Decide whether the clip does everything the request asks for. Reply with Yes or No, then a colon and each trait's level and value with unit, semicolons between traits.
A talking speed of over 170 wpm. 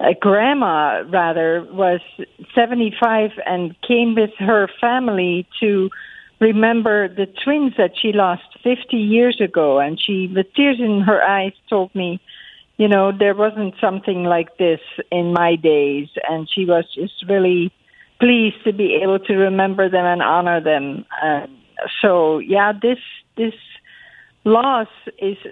No: average, 145 wpm